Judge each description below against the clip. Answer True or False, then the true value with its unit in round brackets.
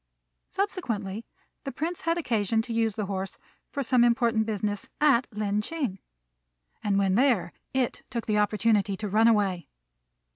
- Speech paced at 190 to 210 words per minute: False (150 wpm)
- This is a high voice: True (220 Hz)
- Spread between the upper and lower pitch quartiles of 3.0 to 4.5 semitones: True (3.4 semitones)